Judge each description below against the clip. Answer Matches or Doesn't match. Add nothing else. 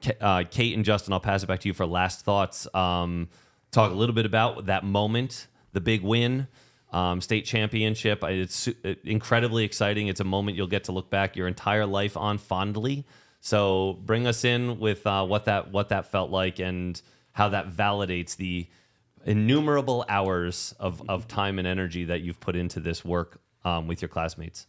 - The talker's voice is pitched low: Matches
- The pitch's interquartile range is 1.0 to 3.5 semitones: Matches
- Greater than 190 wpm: Doesn't match